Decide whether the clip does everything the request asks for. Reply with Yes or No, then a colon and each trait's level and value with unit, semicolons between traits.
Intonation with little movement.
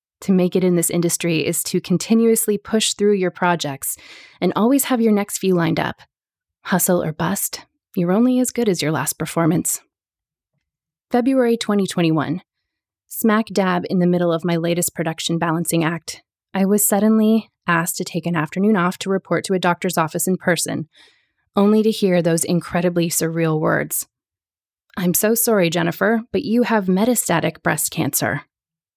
No: average, 3.7 semitones